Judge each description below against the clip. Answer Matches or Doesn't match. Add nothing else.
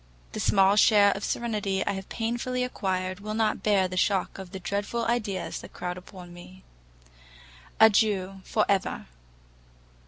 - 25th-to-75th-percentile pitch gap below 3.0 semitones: Matches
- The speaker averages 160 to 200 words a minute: Doesn't match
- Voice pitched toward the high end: Matches